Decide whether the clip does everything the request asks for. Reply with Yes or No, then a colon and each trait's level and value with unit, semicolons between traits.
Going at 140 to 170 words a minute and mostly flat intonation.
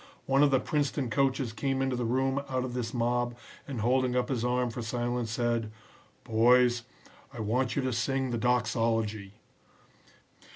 Yes: average, 165 wpm; narrow, 2.1 semitones